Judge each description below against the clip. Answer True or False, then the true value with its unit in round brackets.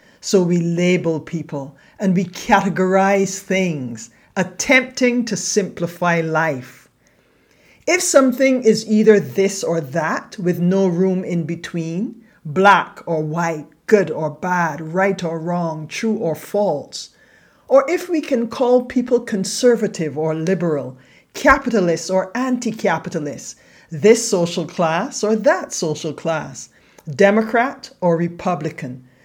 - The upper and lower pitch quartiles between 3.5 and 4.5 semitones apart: False (5.1 semitones)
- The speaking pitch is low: False (185 Hz)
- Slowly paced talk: True (120 wpm)